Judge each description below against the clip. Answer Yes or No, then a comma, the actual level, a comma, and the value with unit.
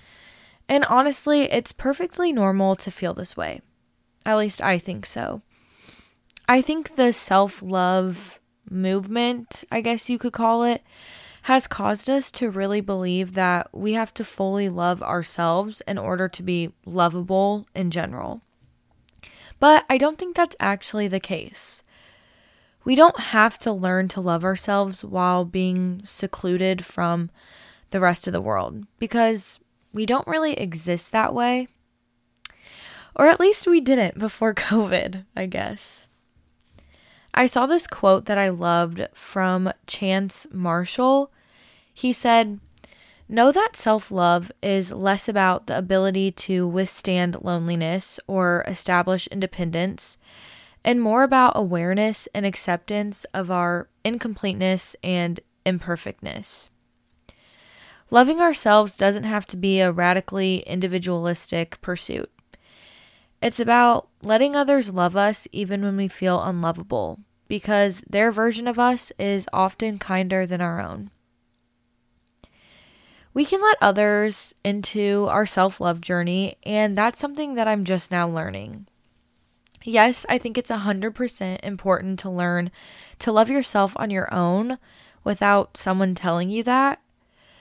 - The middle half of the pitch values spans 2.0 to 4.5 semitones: Yes, average, 4.0 semitones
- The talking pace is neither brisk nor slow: No, slow, 130 wpm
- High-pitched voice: Yes, high, 195 Hz